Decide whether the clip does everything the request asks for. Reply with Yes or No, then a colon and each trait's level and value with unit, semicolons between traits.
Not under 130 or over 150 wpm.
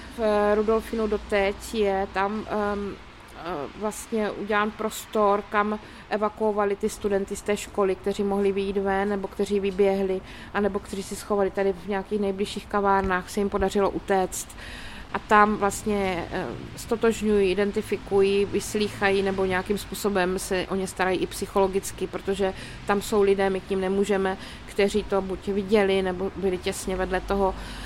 Yes: average, 145 wpm